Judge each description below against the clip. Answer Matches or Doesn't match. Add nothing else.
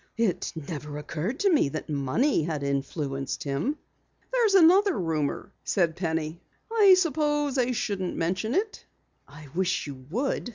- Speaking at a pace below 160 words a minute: Matches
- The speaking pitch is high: Doesn't match